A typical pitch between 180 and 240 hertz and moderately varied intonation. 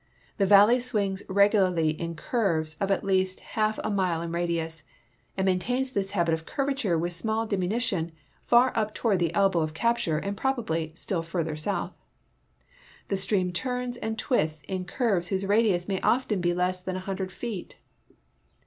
Yes: high, 190 Hz; average, 4.1 semitones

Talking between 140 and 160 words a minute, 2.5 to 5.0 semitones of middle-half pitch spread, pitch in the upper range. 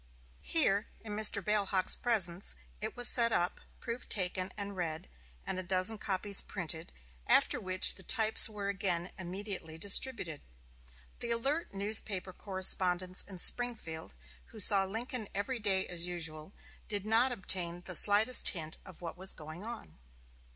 Yes: average, 150 wpm; average, 3.4 semitones; high, 195 Hz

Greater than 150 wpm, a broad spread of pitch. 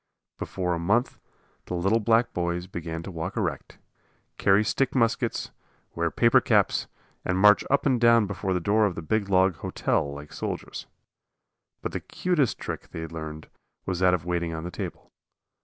No: average, 175 wpm; average, 4.3 semitones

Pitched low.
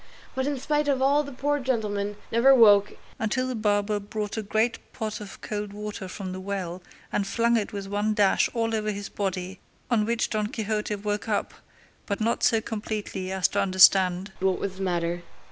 No: high, 210 Hz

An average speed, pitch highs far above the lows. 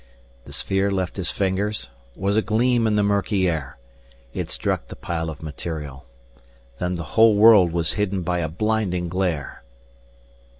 No: average, 160 wpm; average, 3.7 semitones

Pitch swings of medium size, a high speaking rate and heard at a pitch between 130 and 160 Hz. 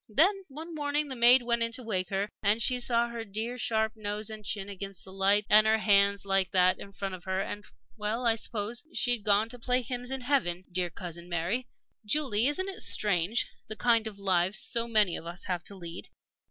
No: average, 3.8 semitones; fast, 220 wpm; high, 215 Hz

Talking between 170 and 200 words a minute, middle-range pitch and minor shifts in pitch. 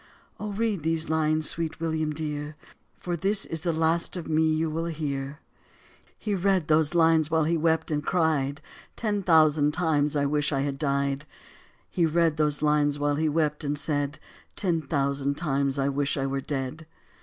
Yes: average, 180 wpm; medium, 155 Hz; narrow, 2.2 semitones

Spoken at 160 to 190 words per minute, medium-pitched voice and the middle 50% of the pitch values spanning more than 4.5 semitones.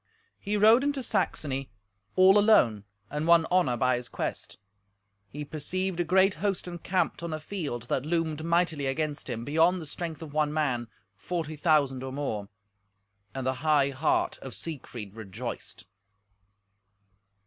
No: average, 150 wpm; medium, 155 Hz; average, 4.9 semitones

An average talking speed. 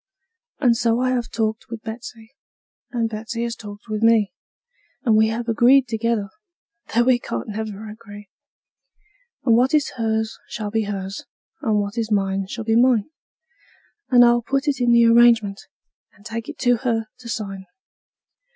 Yes: average, 165 wpm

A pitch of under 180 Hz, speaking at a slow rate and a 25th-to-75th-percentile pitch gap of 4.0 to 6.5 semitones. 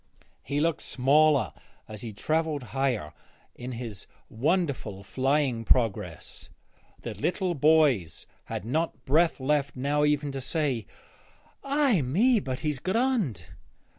Yes: medium, 140 Hz; slow, 120 wpm; average, 4.5 semitones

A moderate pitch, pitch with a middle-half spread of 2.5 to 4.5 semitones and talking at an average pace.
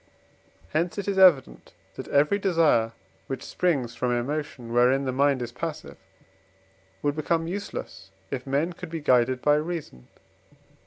No: medium, 145 Hz; average, 4.9 semitones; average, 145 wpm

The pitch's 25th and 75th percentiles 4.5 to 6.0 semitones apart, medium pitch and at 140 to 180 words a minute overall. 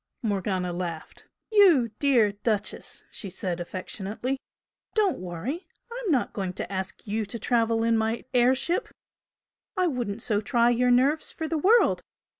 No: wide, 5.6 semitones; high, 230 Hz; average, 150 wpm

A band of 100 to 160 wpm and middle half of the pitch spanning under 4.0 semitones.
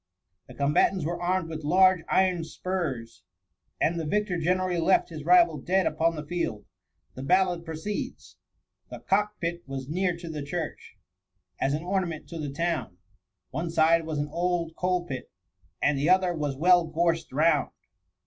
No: average, 170 wpm; average, 2.8 semitones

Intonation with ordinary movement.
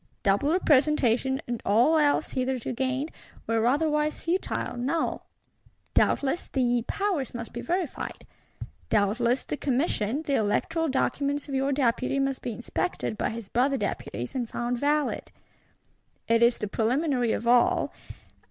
Yes: average, 3.7 semitones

